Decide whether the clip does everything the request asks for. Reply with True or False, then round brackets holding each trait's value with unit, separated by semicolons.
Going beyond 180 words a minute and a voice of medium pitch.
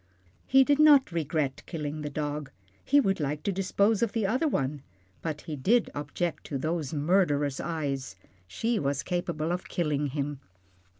False (165 wpm; 155 Hz)